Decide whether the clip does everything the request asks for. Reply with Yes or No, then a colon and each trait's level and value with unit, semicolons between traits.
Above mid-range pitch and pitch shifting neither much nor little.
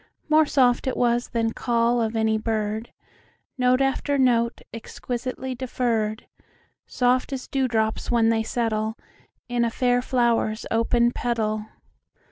No: high, 235 Hz; narrow, 1.9 semitones